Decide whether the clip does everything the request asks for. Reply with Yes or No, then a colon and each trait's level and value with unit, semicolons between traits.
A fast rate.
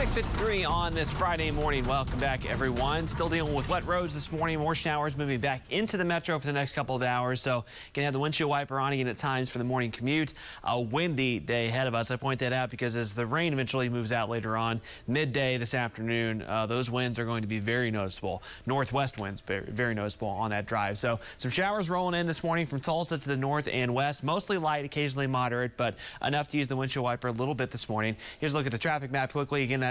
Yes: fast, 240 wpm